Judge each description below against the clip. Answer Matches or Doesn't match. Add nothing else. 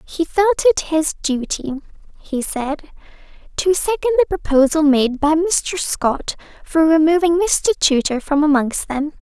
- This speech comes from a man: Doesn't match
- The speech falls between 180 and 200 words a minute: Doesn't match